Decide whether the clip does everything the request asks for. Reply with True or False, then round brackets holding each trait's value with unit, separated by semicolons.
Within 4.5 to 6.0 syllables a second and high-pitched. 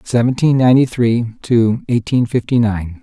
False (4.7 syllables/s; 120 Hz)